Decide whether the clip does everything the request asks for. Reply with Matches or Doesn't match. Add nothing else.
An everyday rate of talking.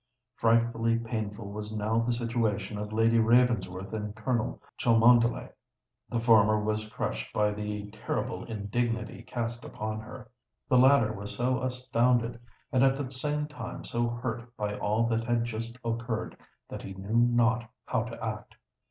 Matches